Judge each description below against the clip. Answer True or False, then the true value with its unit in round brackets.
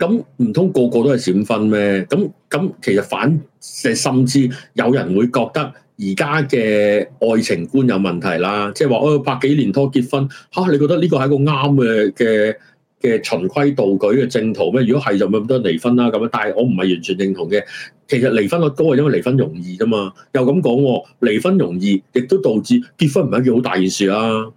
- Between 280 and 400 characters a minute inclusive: True (300 characters per minute)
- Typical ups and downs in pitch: False (5.9 semitones)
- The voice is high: False (125 Hz)